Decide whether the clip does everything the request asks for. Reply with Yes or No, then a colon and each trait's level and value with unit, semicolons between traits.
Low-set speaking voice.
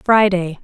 No: high, 190 Hz